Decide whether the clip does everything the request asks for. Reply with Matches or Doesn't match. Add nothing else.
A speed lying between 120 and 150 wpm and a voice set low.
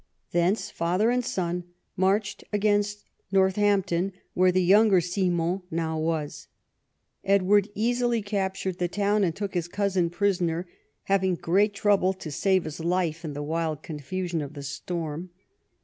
Doesn't match